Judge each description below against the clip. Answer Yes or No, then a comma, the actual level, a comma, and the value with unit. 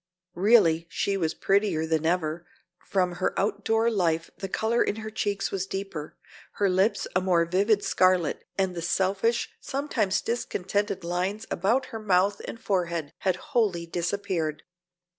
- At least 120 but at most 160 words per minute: Yes, average, 145 wpm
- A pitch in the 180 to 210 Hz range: Yes, high, 190 Hz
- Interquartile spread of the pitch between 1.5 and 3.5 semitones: Yes, average, 3.2 semitones